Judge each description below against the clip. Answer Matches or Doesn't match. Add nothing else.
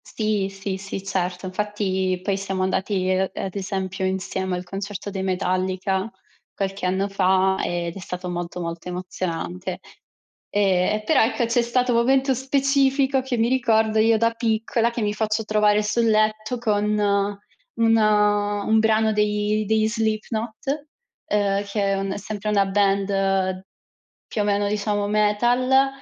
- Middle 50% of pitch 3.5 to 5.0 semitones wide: Doesn't match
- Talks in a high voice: Matches